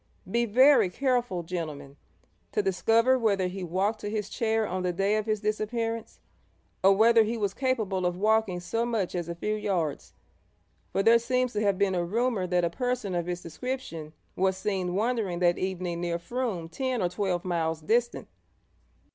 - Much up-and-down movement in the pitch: No, average, 4.3 semitones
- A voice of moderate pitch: No, high, 200 Hz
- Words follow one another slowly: No, average, 180 wpm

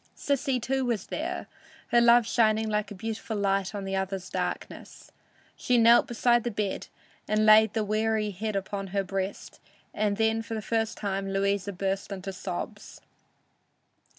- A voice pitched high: Yes, high, 215 Hz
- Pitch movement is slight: Yes, narrow, 2.3 semitones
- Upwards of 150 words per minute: Yes, average, 160 wpm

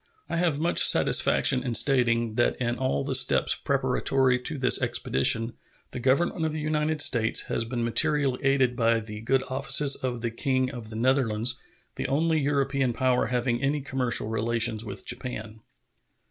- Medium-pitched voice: No, low, 125 Hz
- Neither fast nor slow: Yes, average, 165 wpm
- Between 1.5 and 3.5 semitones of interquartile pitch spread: Yes, average, 2.9 semitones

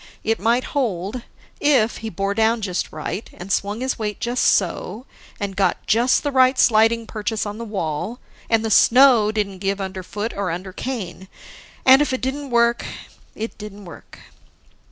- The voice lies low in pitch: No, high, 220 Hz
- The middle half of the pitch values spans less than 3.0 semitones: No, average, 3.4 semitones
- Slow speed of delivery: No, average, 165 wpm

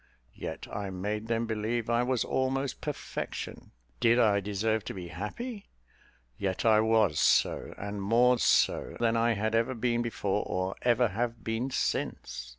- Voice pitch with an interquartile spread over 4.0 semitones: No, narrow, 2.6 semitones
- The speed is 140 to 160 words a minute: Yes, average, 155 wpm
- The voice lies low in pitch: Yes, low, 115 Hz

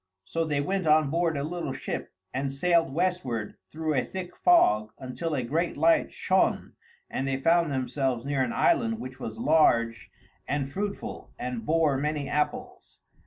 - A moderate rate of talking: Yes, average, 165 wpm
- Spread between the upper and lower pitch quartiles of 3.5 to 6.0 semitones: Yes, average, 4.1 semitones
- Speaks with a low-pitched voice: No, medium, 150 Hz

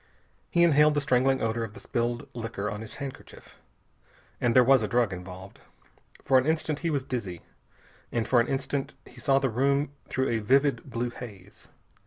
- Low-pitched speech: Yes, low, 125 Hz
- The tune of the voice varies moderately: Yes, average, 3.5 semitones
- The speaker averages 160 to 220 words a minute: Yes, average, 185 wpm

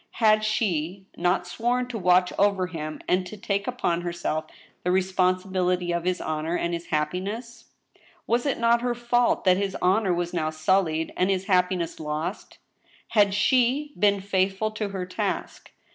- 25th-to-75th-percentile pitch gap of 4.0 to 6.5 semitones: No, average, 3.4 semitones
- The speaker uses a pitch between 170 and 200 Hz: Yes, medium, 185 Hz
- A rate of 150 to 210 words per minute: Yes, average, 165 wpm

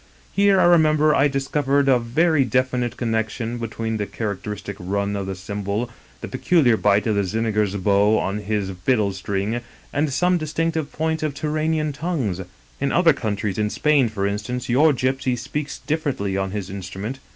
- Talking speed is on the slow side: No, average, 165 wpm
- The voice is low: Yes, low, 120 Hz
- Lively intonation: Yes, wide, 6.3 semitones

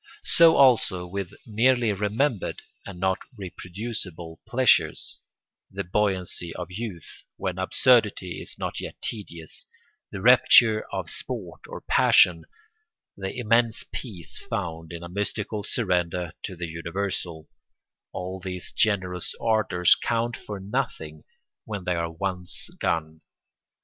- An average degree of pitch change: Yes, average, 3.8 semitones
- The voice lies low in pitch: Yes, very low, 95 Hz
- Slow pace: Yes, slow, 120 wpm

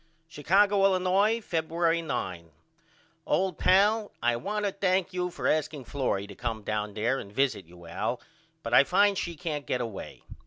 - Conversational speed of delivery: Yes, average, 165 wpm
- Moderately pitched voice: Yes, medium, 160 Hz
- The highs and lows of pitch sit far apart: Yes, wide, 8.6 semitones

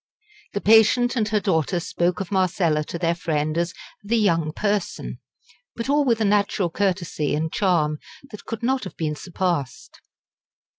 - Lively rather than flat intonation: No, average, 4.5 semitones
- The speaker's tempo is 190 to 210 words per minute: No, average, 160 wpm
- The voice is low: No, medium, 185 Hz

